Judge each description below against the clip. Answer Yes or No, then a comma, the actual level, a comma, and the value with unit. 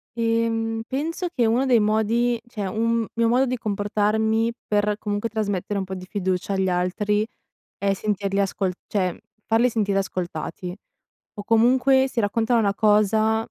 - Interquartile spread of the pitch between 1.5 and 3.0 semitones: Yes, narrow, 2.5 semitones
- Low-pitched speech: No, high, 215 Hz